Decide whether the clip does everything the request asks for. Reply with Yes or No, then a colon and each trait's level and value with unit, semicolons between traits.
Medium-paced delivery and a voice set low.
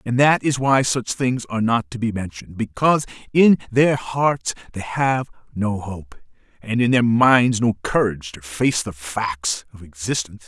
Yes: average, 180 wpm; low, 115 Hz